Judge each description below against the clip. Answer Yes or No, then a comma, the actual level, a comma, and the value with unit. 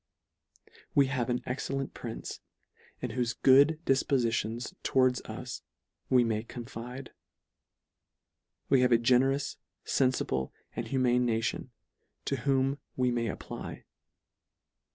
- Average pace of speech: No, slow, 110 wpm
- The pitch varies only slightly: Yes, narrow, 2.3 semitones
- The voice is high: No, low, 125 Hz